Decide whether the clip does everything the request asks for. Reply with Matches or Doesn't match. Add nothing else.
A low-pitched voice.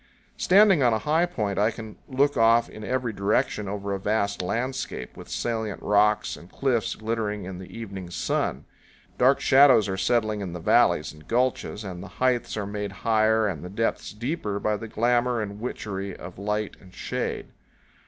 Matches